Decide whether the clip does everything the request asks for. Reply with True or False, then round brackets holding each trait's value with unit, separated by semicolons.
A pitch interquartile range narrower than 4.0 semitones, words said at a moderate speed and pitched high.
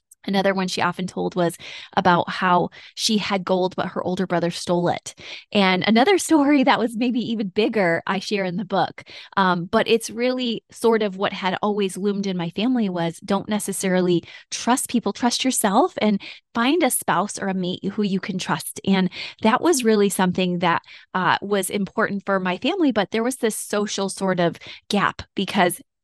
True (3.6 semitones; 190 wpm; 200 Hz)